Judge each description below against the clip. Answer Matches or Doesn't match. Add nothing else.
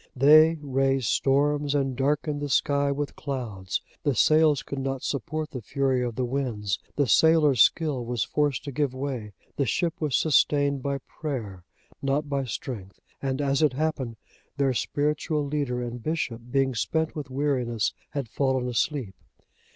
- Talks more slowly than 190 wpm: Matches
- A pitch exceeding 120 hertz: Matches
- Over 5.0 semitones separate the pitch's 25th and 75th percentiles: Doesn't match